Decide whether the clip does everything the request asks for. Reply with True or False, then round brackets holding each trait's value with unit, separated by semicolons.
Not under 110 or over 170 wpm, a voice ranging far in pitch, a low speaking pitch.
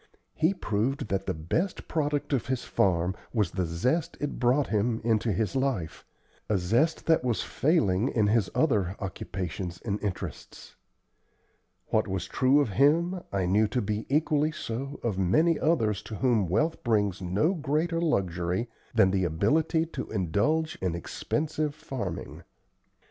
True (150 wpm; 7.7 semitones; 115 Hz)